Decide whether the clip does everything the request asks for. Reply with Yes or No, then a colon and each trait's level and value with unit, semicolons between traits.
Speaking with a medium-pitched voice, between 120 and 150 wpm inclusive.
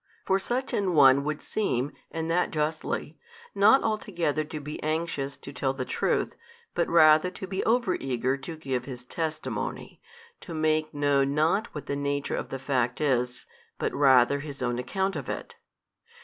No: medium, 150 Hz; average, 170 wpm